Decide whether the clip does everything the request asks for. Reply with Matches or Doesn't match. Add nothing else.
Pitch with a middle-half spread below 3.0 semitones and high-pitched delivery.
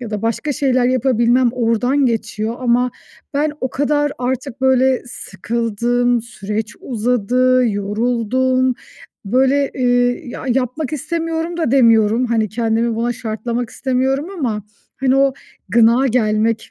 Matches